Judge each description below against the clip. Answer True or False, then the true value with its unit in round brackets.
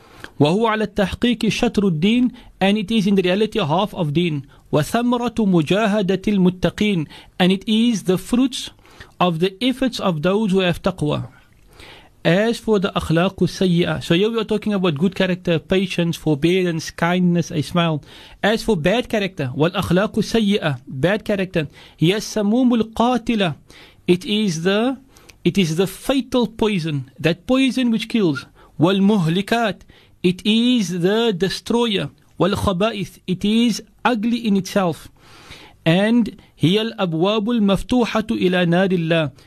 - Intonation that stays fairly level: False (4.2 semitones)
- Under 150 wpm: True (135 wpm)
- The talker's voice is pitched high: True (195 Hz)